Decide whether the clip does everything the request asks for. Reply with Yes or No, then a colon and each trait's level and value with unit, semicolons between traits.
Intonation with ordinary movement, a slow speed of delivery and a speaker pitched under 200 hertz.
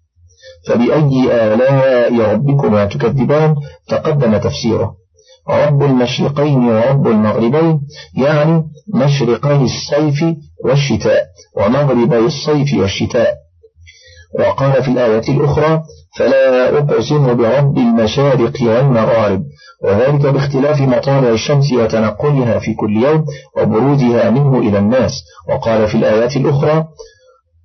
No: average, 4.8 semitones; average, 90 wpm; low, 135 Hz